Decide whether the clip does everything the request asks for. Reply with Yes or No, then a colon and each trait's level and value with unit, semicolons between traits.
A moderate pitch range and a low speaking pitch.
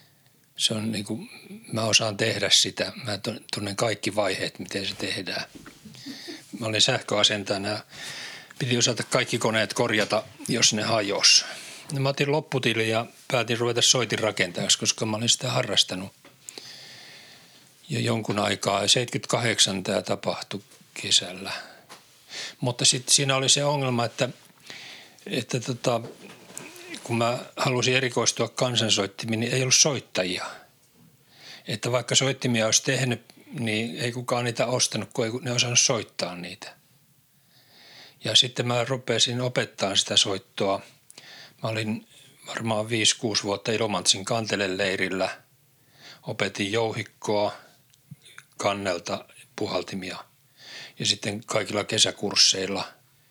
Yes: average, 3.5 semitones; low, 115 Hz